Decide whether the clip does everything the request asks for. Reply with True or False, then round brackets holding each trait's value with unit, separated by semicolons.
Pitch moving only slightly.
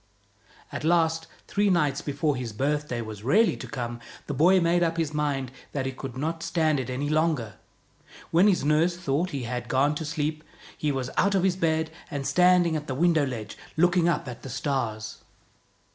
False (4.1 semitones)